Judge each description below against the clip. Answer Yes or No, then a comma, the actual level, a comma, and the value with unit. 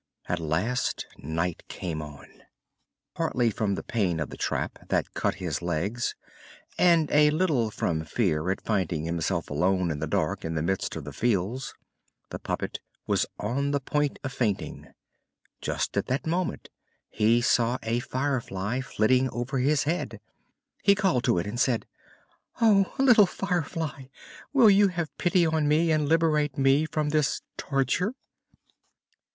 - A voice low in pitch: Yes, low, 125 Hz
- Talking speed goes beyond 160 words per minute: No, average, 155 wpm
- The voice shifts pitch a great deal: Yes, wide, 8.6 semitones